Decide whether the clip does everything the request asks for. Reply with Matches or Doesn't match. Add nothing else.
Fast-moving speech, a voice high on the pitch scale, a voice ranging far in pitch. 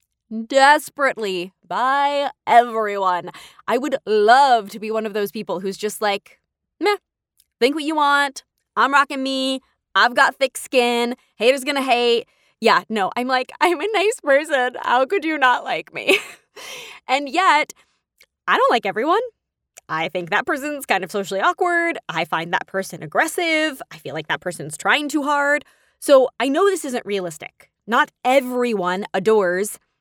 Doesn't match